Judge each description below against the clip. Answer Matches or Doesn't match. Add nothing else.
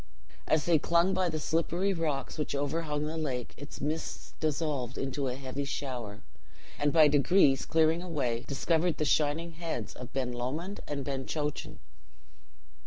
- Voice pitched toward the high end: Doesn't match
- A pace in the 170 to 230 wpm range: Doesn't match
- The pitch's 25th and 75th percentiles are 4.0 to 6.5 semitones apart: Doesn't match